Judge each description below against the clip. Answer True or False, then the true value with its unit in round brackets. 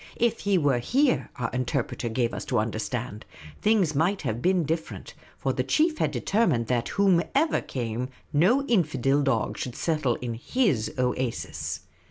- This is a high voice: False (140 Hz)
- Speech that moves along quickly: False (155 wpm)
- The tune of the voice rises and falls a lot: True (8.5 semitones)